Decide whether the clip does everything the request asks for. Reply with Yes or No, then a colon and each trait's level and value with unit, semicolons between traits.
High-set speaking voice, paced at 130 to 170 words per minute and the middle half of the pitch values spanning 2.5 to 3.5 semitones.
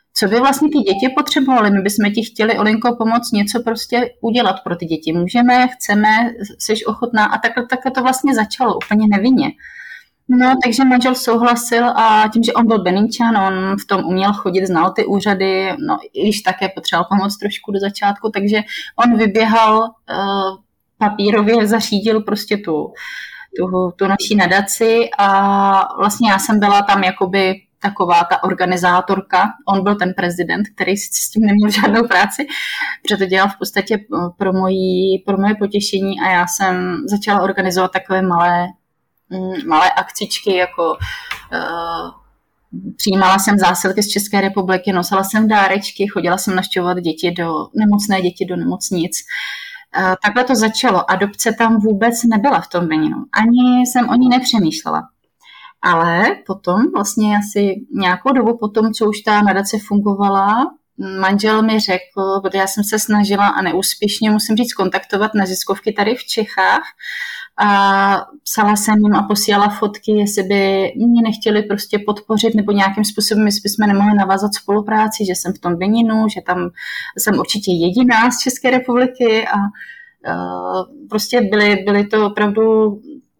Yes: high, 210 Hz; average, 150 wpm; average, 2.9 semitones